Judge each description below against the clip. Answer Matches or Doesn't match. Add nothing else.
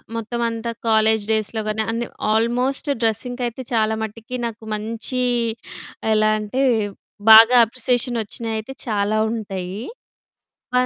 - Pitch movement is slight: Matches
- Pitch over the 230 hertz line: Doesn't match